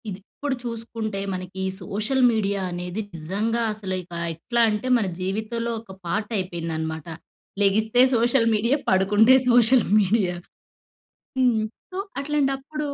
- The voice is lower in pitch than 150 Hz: No, high, 215 Hz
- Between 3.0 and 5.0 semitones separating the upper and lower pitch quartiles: Yes, average, 4.0 semitones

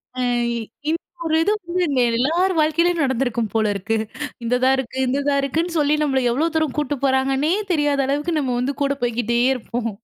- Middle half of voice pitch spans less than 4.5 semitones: Yes, average, 4.1 semitones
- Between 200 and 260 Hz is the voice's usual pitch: No, very high, 275 Hz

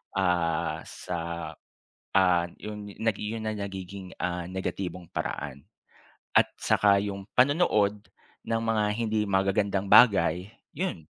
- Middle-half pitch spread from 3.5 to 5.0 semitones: No, average, 3.1 semitones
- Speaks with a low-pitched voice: Yes, low, 100 Hz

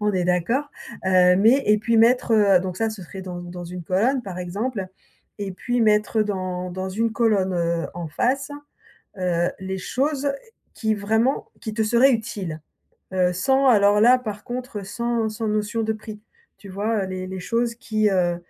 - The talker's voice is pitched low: No, high, 210 Hz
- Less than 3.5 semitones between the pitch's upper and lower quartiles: No, average, 3.8 semitones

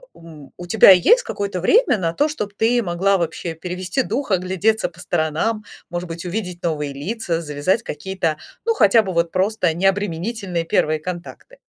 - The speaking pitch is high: No, medium, 180 Hz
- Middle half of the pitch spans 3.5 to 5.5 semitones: Yes, average, 4.2 semitones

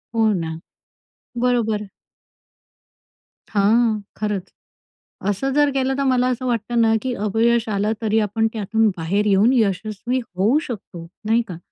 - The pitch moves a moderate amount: Yes, average, 3.0 semitones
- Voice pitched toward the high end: Yes, high, 220 Hz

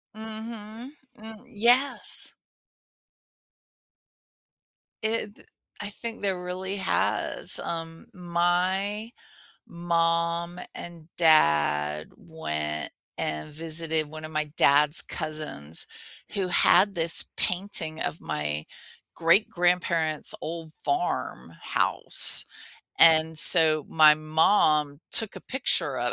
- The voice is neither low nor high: Yes, medium, 170 Hz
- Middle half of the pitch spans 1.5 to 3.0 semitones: No, average, 4.0 semitones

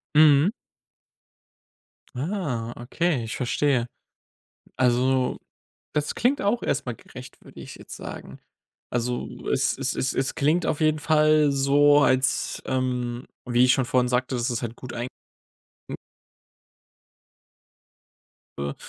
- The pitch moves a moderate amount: Yes, average, 3.4 semitones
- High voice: No, low, 130 Hz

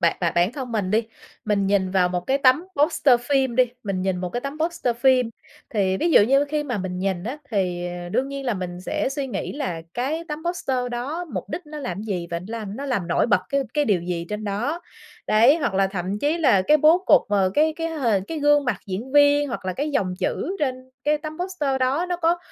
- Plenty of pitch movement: Yes, wide, 7.2 semitones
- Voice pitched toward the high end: Yes, very high, 250 Hz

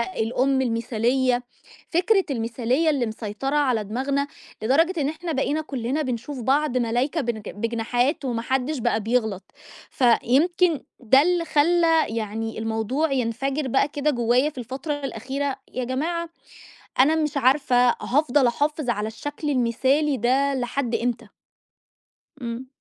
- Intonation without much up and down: No, average, 3.8 semitones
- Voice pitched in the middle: No, very high, 260 Hz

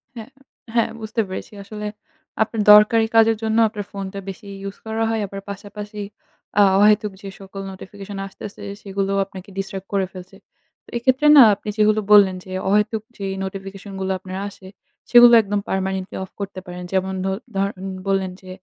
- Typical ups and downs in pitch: No, narrow, 1.9 semitones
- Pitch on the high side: Yes, high, 200 Hz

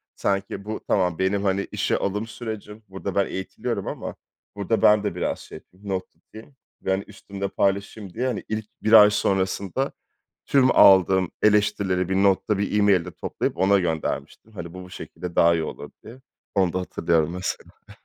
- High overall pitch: No, low, 100 Hz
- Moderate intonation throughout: No, narrow, 2.2 semitones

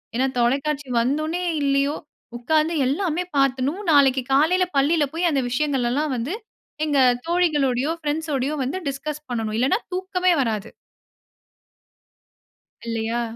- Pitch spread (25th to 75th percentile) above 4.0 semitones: No, average, 3.5 semitones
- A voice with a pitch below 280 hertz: No, very high, 285 Hz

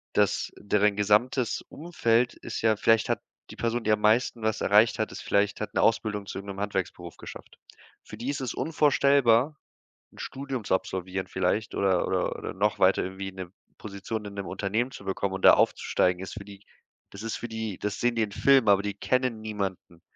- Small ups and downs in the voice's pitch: No, average, 3.0 semitones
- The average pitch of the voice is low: Yes, low, 105 Hz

